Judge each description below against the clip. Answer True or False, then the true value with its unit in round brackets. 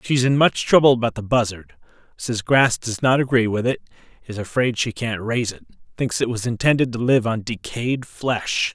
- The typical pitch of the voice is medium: False (120 Hz)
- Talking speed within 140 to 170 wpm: False (205 wpm)